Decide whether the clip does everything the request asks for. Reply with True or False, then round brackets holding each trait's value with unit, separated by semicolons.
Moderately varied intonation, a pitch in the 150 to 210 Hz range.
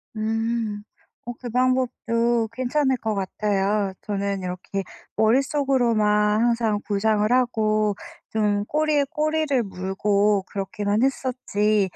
False (3.3 semitones; 220 Hz)